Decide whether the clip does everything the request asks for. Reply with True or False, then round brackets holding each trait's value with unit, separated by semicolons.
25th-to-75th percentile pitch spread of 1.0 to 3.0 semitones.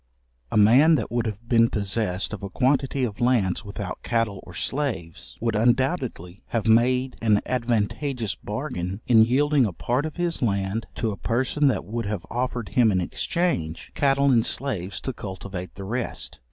False (4.3 semitones)